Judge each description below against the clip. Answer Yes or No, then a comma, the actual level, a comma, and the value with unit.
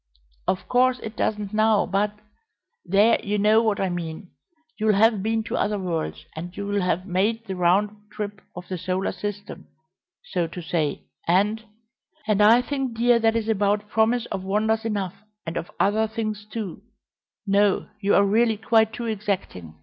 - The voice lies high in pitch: Yes, high, 210 Hz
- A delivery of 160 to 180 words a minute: Yes, average, 170 wpm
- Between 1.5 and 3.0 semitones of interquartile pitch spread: Yes, narrow, 2.5 semitones